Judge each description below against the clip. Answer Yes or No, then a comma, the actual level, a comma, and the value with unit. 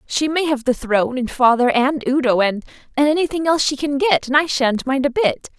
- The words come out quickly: Yes, fast, 225 wpm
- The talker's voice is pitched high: Yes, very high, 270 Hz